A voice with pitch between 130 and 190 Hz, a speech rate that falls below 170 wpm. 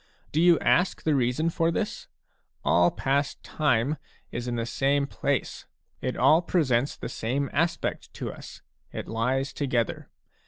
Yes: medium, 140 Hz; average, 150 wpm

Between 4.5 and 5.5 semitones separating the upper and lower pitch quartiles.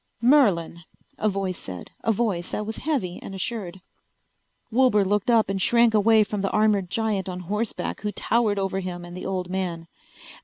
No: average, 3.3 semitones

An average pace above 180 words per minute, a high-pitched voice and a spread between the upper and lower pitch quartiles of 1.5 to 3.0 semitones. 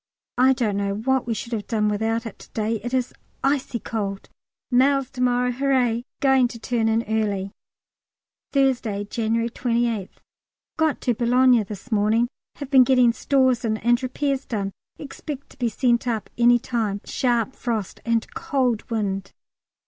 No: average, 160 wpm; high, 235 Hz; average, 2.7 semitones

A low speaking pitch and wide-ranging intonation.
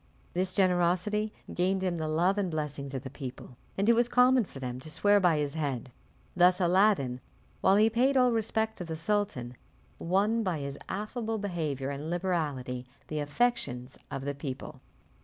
No: medium, 175 Hz; wide, 6.5 semitones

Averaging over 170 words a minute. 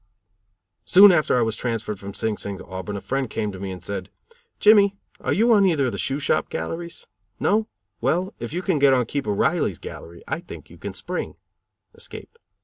Yes: fast, 205 wpm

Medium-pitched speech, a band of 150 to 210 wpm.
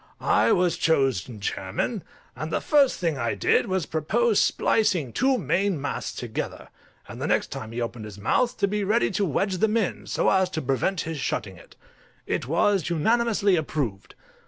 Yes: medium, 170 Hz; average, 180 wpm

